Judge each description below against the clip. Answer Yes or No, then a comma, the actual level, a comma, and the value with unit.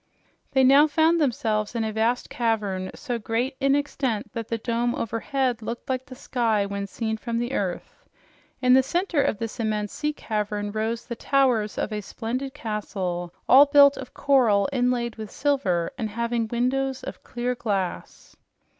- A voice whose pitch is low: No, high, 235 Hz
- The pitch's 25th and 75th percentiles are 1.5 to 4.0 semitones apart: Yes, average, 3.7 semitones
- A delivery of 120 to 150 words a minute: No, average, 165 wpm